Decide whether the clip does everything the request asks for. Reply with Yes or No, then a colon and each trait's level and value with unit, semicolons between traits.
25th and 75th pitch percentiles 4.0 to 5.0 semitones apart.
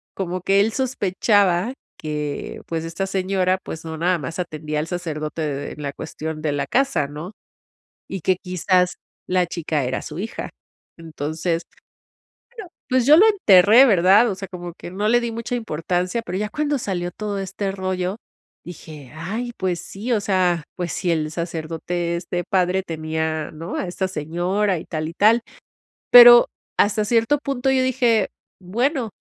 Yes: average, 4.5 semitones